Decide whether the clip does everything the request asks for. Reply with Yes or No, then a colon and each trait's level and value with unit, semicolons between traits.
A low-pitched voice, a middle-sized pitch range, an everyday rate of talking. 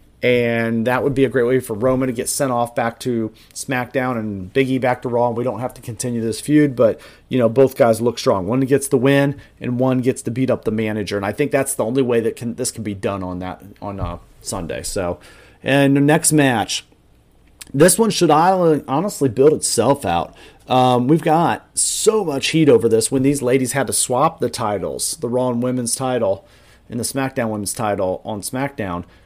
No: low, 125 Hz; average, 3.4 semitones; fast, 215 wpm